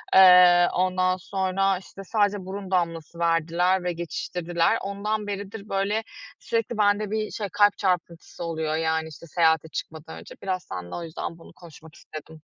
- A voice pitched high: No, medium, 180 Hz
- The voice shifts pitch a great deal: No, average, 3.1 semitones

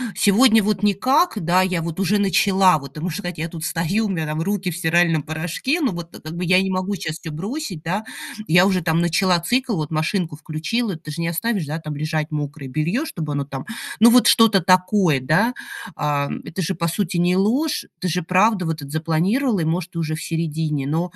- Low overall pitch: No, medium, 175 Hz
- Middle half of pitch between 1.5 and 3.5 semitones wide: No, average, 4.0 semitones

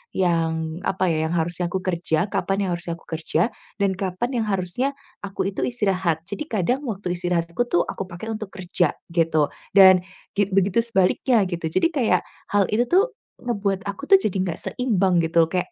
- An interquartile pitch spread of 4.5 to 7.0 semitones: No, average, 3.6 semitones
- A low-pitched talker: No, high, 190 Hz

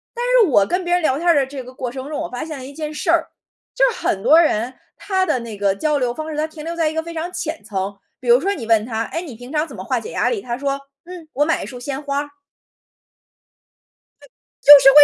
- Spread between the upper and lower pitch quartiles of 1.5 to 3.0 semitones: No, average, 4.5 semitones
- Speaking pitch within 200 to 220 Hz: No, very high, 285 Hz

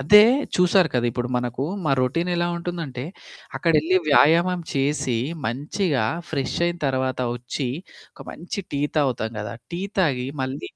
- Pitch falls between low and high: Yes, medium, 145 Hz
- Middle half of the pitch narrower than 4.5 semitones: No, average, 5.1 semitones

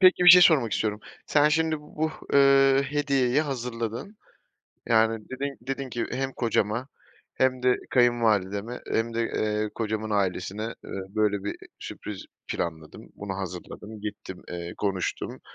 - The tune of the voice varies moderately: Yes, average, 4.6 semitones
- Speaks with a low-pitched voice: Yes, low, 115 Hz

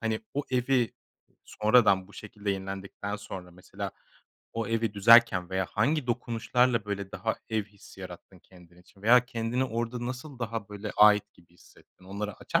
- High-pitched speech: No, low, 110 Hz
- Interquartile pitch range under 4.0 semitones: Yes, average, 3.3 semitones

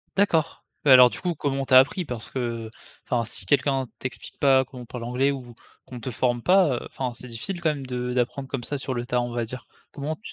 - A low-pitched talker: Yes, low, 130 Hz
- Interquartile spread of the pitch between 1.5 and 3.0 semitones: Yes, narrow, 2.5 semitones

